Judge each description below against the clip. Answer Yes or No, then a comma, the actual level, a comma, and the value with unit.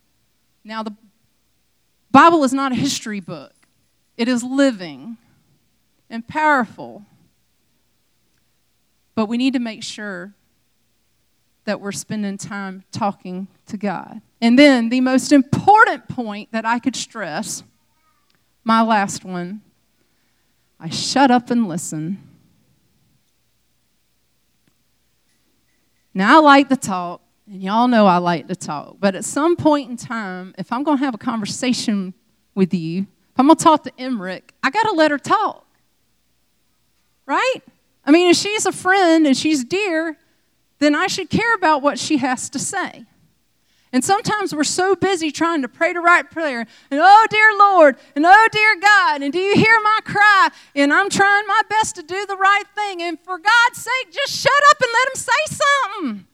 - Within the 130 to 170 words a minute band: Yes, average, 160 wpm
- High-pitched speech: Yes, very high, 270 Hz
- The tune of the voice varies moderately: No, wide, 8.5 semitones